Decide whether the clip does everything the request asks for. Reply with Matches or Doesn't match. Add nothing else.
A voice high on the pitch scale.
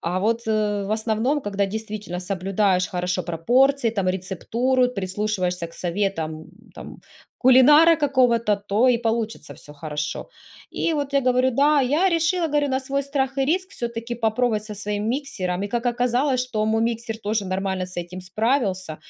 Matches